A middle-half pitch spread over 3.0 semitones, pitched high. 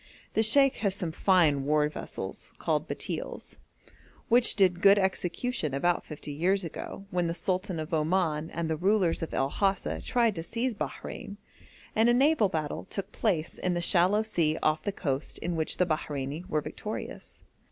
No: average, 4.4 semitones; medium, 175 Hz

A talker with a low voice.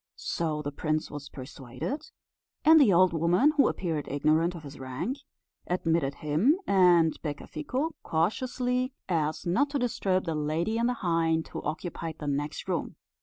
No: medium, 165 Hz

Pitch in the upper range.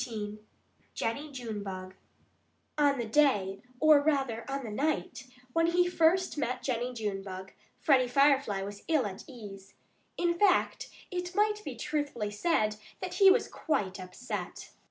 Yes: very high, 255 Hz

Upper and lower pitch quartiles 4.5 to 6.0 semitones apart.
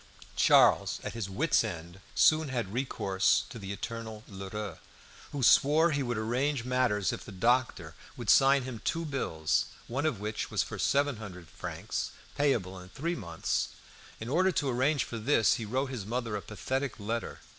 Yes: average, 5.1 semitones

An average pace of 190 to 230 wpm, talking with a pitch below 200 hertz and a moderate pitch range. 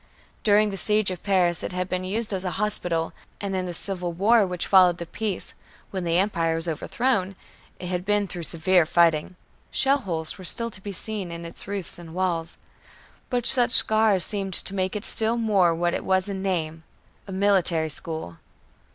Yes: average, 195 wpm; medium, 185 Hz; average, 3.0 semitones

